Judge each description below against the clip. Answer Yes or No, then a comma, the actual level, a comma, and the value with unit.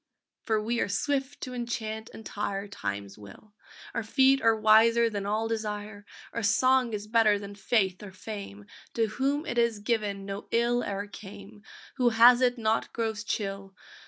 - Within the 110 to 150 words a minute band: No, average, 170 wpm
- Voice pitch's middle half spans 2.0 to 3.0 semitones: Yes, narrow, 2.6 semitones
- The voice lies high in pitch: Yes, high, 215 Hz